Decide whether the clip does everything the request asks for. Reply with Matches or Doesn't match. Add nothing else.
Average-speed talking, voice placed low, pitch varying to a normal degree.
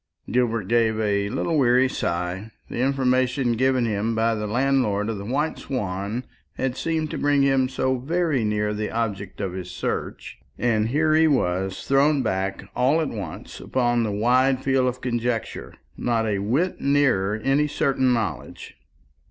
Matches